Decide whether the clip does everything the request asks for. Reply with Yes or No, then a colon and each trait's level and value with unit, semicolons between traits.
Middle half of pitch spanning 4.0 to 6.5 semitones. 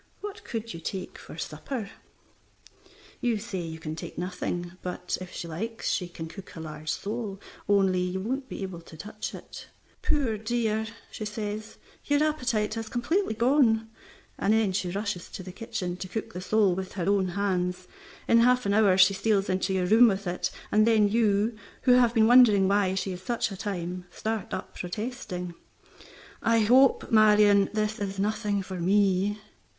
No: average, 3.4 semitones